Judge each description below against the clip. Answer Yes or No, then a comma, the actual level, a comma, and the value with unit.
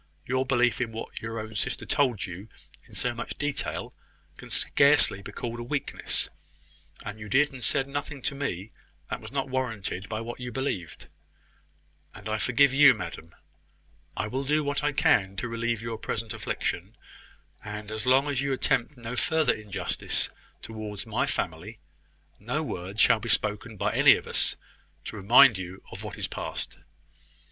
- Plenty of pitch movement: No, average, 4.1 semitones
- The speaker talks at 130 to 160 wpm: No, average, 170 wpm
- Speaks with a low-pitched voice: Yes, low, 115 Hz